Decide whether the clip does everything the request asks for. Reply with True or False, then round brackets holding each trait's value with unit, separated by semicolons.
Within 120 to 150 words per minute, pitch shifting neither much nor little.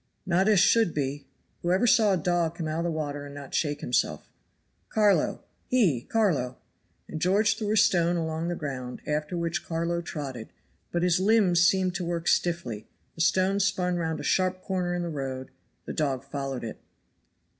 False (185 wpm; 4.2 semitones)